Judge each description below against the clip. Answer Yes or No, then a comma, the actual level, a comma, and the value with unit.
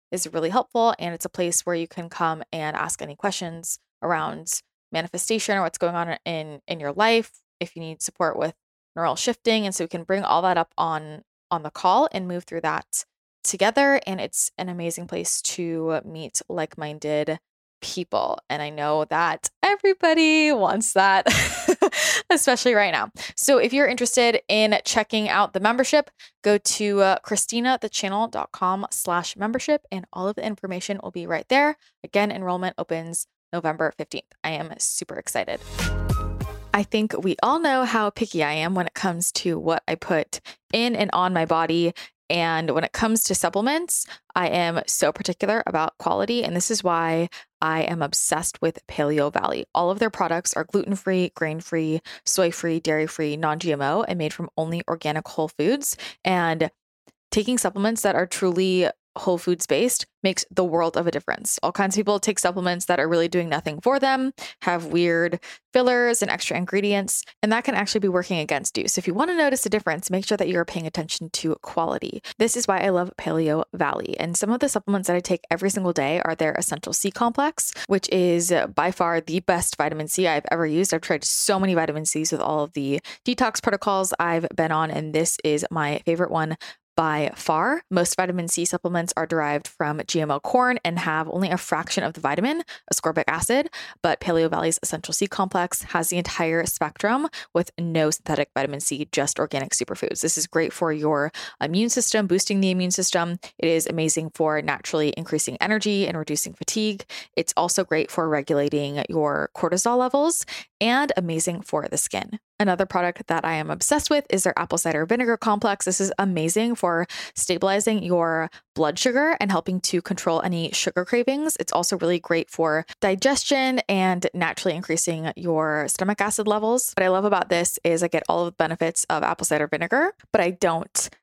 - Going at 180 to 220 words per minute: Yes, average, 190 wpm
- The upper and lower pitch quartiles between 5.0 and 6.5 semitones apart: No, average, 4.2 semitones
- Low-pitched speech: No, medium, 180 Hz